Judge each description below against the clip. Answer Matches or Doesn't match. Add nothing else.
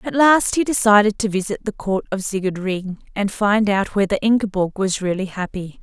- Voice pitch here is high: Matches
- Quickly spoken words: Doesn't match